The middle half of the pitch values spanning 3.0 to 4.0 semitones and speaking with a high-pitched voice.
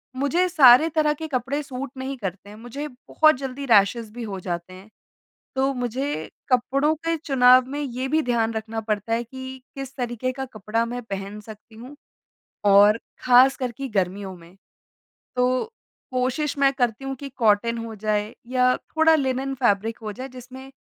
Yes: average, 3.6 semitones; very high, 250 Hz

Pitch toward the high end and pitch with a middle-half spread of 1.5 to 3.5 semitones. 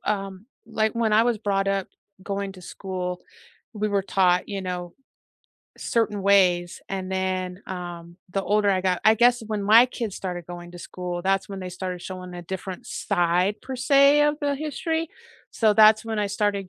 Yes: high, 195 Hz; average, 3.1 semitones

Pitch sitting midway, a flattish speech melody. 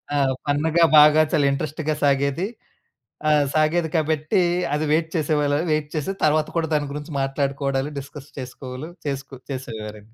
Yes: medium, 145 Hz; narrow, 2.1 semitones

